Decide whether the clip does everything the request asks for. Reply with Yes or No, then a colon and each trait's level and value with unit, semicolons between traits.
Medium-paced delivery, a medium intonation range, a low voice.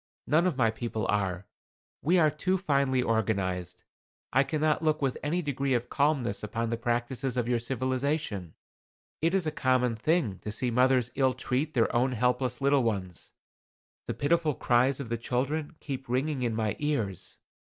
Yes: average, 170 wpm; average, 4.0 semitones; low, 130 Hz